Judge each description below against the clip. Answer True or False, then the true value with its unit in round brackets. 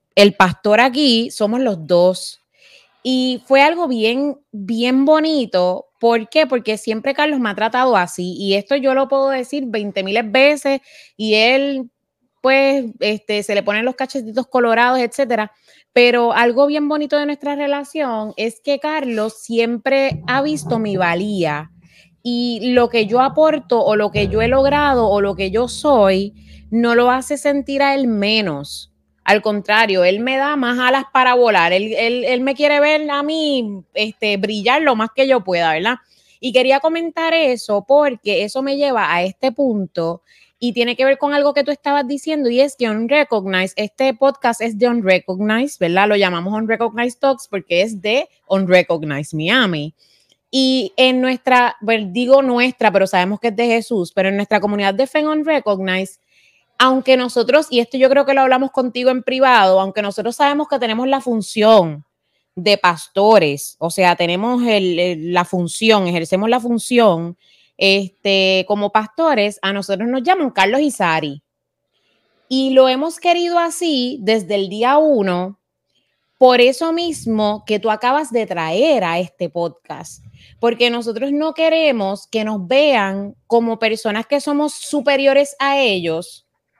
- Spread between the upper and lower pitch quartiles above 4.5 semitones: True (5.1 semitones)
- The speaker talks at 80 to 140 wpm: False (170 wpm)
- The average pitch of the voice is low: False (235 Hz)